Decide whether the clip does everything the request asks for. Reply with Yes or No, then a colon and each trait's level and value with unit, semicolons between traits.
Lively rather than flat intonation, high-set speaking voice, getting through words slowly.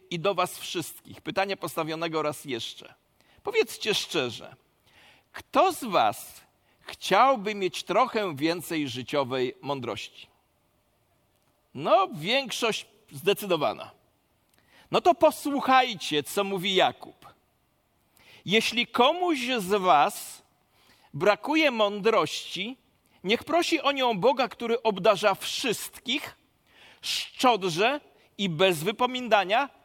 Yes: wide, 6.6 semitones; high, 215 Hz; slow, 90 wpm